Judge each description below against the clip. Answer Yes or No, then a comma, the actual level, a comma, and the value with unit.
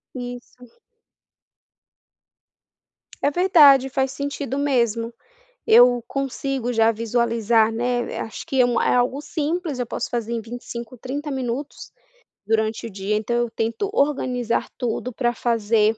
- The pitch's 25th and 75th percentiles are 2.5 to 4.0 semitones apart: Yes, average, 2.9 semitones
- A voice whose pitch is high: Yes, high, 245 Hz